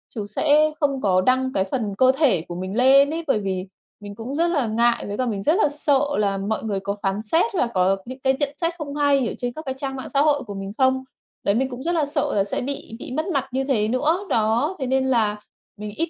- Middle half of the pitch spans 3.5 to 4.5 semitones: No, average, 5.3 semitones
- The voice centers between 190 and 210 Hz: No, very high, 255 Hz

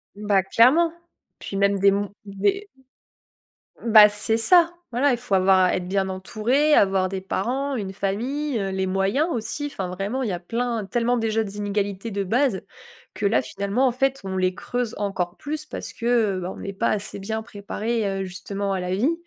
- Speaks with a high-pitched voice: Yes, high, 205 Hz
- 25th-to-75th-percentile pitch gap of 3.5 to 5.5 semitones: Yes, average, 4.2 semitones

